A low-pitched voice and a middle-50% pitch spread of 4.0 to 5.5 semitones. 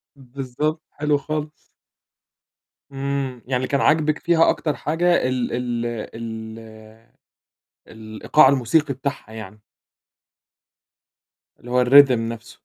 Yes: low, 130 Hz; average, 4.4 semitones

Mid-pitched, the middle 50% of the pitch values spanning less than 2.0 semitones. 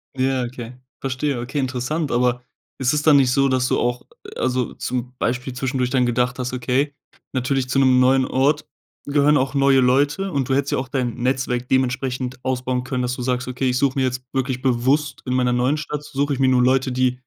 No: low, 130 Hz; narrow, 1.4 semitones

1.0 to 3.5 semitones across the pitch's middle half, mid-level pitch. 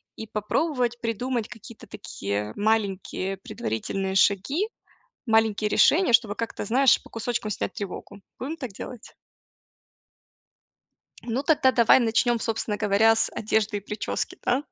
No: average, 3.1 semitones; high, 225 Hz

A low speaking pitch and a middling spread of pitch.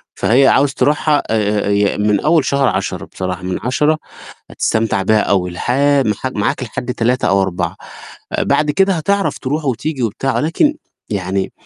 No: low, 120 Hz; wide, 6.3 semitones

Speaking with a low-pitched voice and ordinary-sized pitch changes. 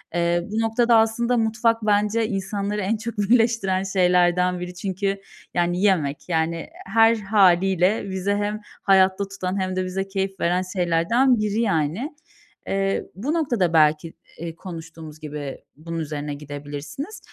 No: high, 190 Hz; average, 3.8 semitones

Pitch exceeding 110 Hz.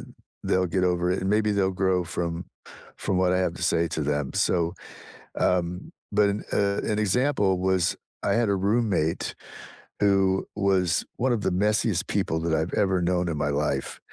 No: very low, 95 Hz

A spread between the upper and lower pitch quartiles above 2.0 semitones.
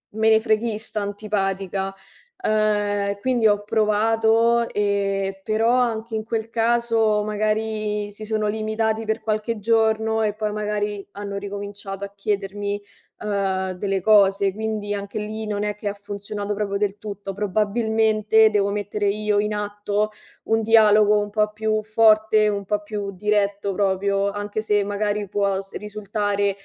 No: narrow, 1.3 semitones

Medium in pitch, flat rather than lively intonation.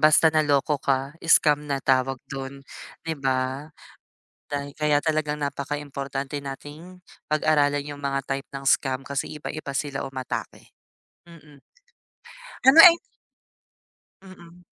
Yes: medium, 145 Hz; narrow, 1.9 semitones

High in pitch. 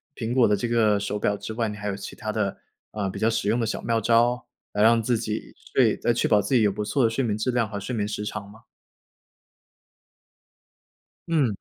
No: low, 110 Hz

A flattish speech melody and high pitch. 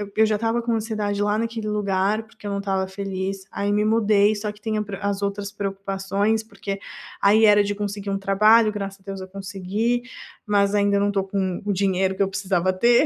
Yes: narrow, 1.4 semitones; high, 200 Hz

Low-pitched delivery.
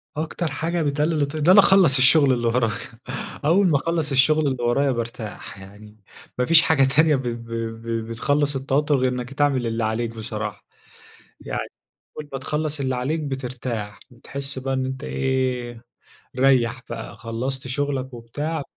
Yes: low, 130 Hz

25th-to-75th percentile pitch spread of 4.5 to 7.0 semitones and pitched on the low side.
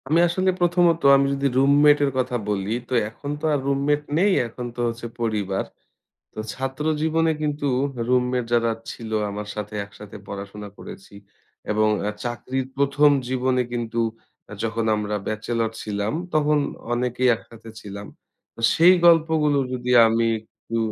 Yes: average, 5.1 semitones; low, 125 Hz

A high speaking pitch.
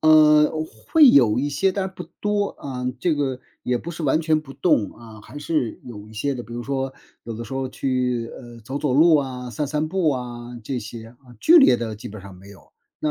No: low, 130 Hz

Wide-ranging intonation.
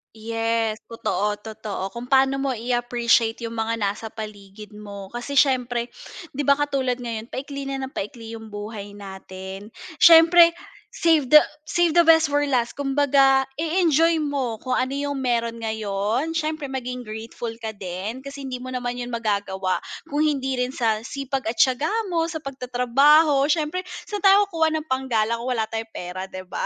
No: average, 4.3 semitones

